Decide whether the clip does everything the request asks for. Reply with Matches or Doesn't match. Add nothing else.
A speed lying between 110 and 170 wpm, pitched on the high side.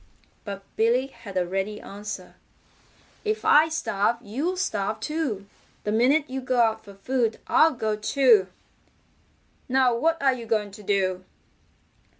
Matches